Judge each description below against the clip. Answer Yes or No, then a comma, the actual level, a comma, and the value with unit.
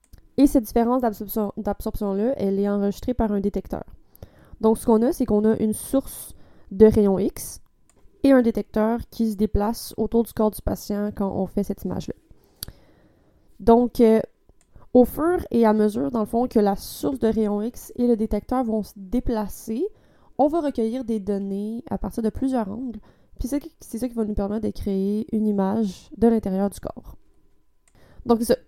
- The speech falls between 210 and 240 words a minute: No, average, 185 wpm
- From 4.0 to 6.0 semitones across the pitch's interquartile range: No, average, 2.7 semitones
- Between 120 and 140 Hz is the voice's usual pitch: No, high, 220 Hz